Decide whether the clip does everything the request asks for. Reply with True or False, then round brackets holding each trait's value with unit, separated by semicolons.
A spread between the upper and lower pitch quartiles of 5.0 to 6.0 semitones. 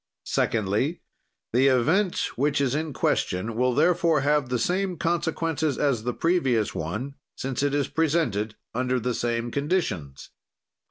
True (5.3 semitones)